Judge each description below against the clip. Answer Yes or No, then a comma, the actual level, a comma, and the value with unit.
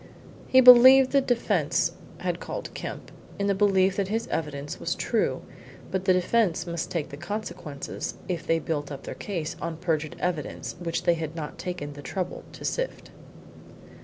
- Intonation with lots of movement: No, average, 4.4 semitones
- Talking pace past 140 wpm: Yes, average, 170 wpm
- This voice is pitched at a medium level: Yes, medium, 175 Hz